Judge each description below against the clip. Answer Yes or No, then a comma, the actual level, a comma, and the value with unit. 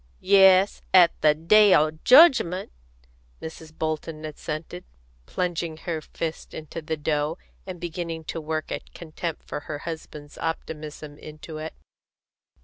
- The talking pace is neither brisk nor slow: No, slow, 130 wpm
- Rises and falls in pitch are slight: Yes, narrow, 1.8 semitones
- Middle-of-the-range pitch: Yes, medium, 160 Hz